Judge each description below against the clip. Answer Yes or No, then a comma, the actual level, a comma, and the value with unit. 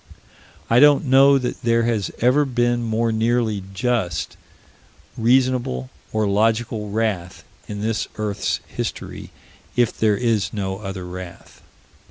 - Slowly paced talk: Yes, slow, 125 wpm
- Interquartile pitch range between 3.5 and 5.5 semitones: No, average, 3.1 semitones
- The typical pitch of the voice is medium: No, low, 110 Hz